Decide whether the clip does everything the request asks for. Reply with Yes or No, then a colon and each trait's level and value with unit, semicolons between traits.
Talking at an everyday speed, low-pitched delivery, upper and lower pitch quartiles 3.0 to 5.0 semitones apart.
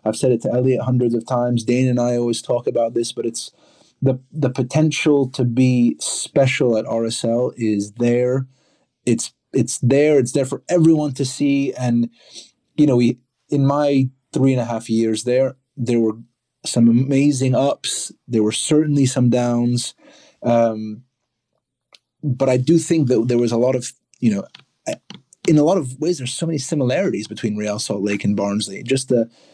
No: average, 180 wpm; low, 125 Hz; narrow, 2.6 semitones